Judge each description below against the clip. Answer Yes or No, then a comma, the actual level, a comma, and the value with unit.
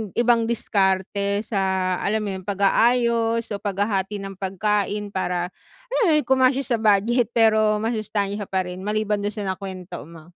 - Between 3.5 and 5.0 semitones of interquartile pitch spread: No, average, 2.8 semitones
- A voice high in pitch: Yes, high, 205 Hz